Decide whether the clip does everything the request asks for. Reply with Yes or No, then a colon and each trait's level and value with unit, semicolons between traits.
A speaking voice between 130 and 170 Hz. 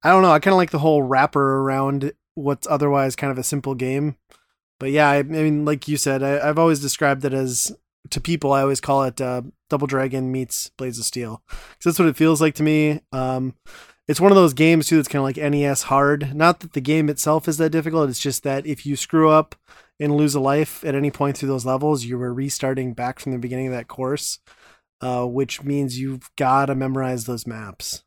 Yes: medium, 140 Hz